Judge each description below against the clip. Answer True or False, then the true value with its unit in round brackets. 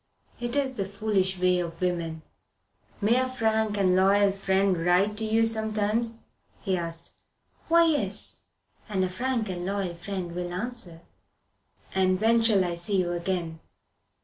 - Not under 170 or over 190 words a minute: False (150 wpm)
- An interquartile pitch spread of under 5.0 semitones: True (3.6 semitones)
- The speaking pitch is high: True (195 Hz)